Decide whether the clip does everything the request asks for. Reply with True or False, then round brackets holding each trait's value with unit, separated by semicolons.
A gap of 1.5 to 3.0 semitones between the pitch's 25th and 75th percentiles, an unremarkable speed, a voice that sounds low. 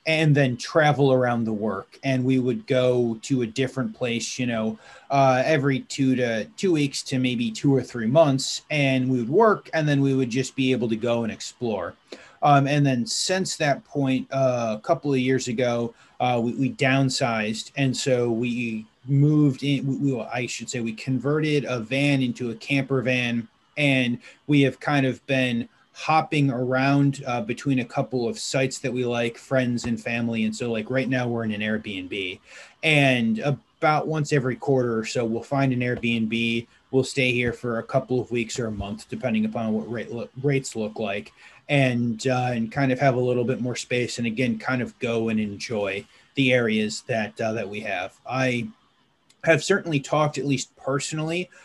True (2.7 semitones; 195 wpm; 130 Hz)